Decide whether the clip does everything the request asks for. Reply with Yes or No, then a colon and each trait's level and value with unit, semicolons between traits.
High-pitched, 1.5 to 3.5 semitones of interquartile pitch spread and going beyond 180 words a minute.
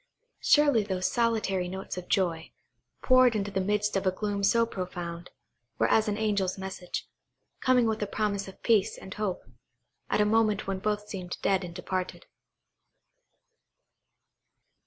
No: high, 200 Hz; narrow, 2.5 semitones; average, 150 wpm